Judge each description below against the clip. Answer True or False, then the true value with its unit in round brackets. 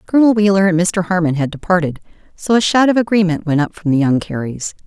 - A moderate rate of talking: False (220 wpm)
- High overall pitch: False (180 Hz)